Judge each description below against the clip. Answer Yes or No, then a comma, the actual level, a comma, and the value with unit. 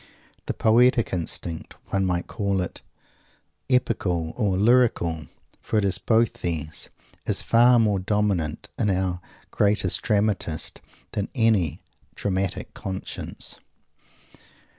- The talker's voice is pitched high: No, low, 100 Hz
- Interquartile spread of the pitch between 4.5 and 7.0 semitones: No, average, 4.0 semitones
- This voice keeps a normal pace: No, slow, 115 wpm